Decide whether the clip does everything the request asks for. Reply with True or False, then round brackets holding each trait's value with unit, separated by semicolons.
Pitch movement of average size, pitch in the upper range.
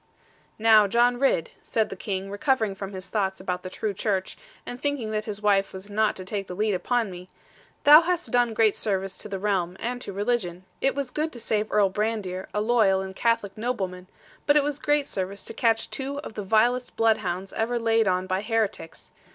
True (3.7 semitones; 210 Hz)